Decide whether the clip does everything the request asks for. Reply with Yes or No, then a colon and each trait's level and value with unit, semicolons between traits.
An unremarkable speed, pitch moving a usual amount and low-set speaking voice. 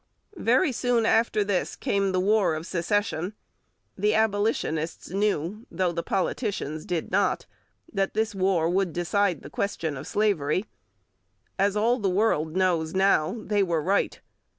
No: average, 145 wpm; average, 3.6 semitones; high, 195 Hz